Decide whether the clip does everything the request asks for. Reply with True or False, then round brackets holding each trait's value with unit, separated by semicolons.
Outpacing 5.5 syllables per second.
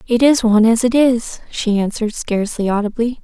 True (5.8 syllables/s)